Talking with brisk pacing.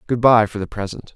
Yes: fast, 260 wpm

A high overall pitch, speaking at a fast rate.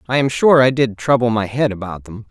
No: low, 120 Hz; fast, 260 wpm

